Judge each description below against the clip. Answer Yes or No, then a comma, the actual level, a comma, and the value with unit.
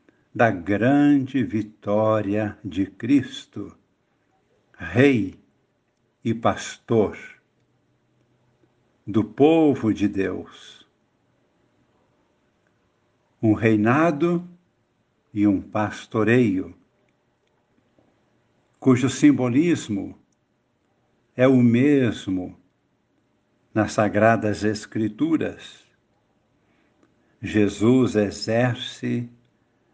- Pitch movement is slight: No, average, 3.2 semitones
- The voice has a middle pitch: No, low, 115 Hz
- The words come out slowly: Yes, slow, 55 wpm